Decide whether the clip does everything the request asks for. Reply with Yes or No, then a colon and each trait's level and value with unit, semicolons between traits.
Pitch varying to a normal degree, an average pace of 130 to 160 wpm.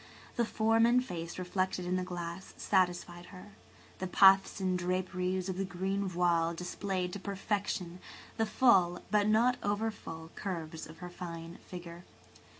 No: narrow, 2.3 semitones; average, 150 wpm